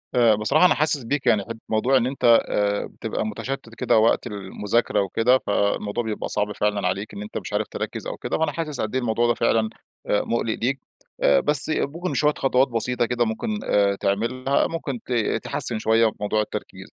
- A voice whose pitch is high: No, low, 115 Hz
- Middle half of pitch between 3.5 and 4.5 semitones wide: Yes, average, 3.9 semitones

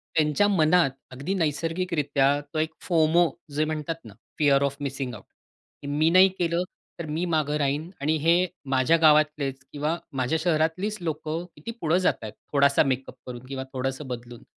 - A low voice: No, medium, 155 Hz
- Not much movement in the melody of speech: No, average, 3.2 semitones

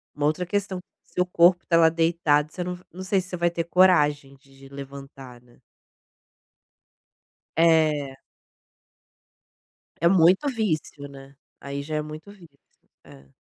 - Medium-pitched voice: Yes, medium, 160 Hz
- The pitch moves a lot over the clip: No, average, 4.3 semitones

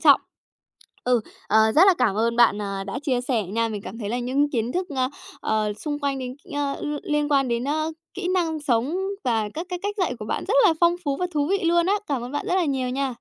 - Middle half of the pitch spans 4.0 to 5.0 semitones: No, wide, 5.5 semitones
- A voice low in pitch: No, very high, 270 Hz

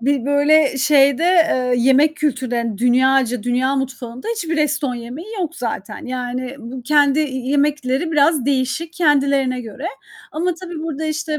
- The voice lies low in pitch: No, very high, 275 Hz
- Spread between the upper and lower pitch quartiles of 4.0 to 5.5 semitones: No, average, 3.4 semitones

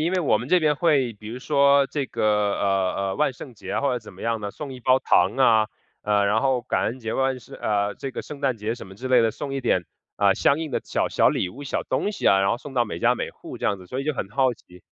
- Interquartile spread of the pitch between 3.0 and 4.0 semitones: No, average, 4.7 semitones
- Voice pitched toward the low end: Yes, low, 125 Hz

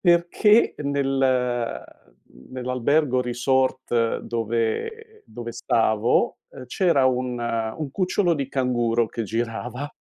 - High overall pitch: No, low, 125 Hz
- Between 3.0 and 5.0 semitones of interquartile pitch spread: Yes, average, 3.3 semitones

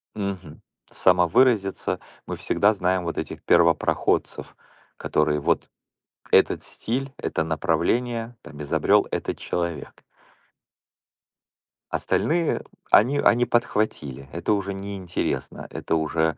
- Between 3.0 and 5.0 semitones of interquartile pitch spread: No, wide, 5.6 semitones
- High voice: No, very low, 95 Hz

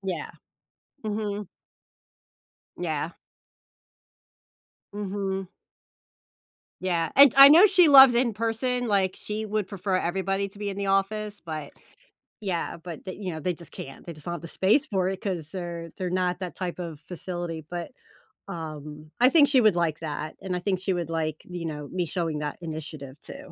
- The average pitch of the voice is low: No, medium, 185 Hz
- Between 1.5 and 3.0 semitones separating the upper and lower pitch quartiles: No, average, 3.8 semitones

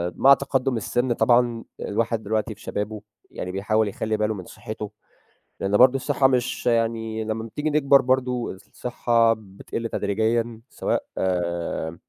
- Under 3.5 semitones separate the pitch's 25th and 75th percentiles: Yes, average, 2.8 semitones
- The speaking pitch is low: Yes, low, 115 Hz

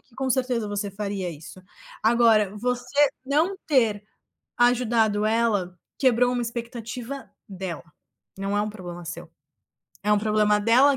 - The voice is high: Yes, high, 220 Hz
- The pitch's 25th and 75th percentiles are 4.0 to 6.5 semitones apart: No, average, 3.3 semitones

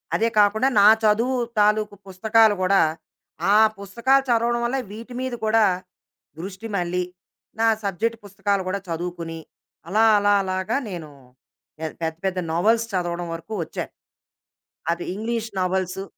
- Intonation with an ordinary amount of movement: Yes, average, 3.7 semitones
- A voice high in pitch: Yes, high, 205 Hz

